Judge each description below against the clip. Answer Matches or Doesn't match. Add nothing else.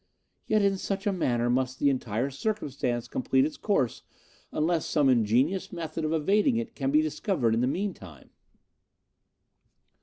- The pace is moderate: Matches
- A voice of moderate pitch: Matches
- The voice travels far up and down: Matches